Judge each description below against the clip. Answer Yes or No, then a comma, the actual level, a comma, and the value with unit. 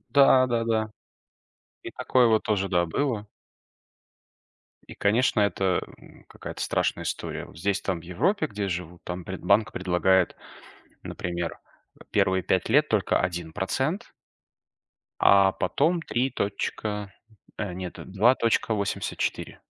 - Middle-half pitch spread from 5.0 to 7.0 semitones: No, average, 4.0 semitones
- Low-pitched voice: Yes, low, 100 Hz